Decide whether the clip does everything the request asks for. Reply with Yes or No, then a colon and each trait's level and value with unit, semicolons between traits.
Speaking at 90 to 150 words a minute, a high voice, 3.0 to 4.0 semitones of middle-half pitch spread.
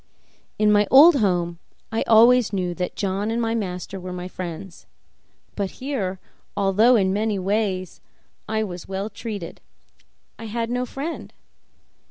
Yes: average, 145 wpm; high, 205 Hz; average, 3.5 semitones